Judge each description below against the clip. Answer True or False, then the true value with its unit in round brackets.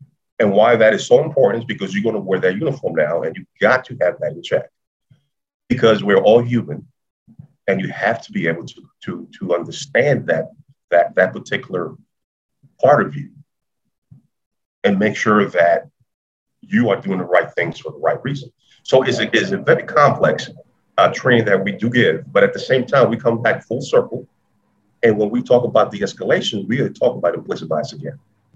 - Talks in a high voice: False (125 Hz)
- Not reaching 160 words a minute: False (200 wpm)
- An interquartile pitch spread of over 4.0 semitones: True (4.8 semitones)